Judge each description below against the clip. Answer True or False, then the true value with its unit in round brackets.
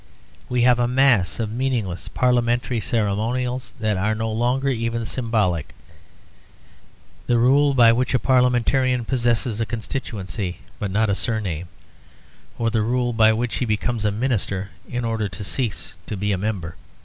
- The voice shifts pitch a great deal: False (2.9 semitones)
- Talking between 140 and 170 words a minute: True (155 wpm)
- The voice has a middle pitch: False (115 Hz)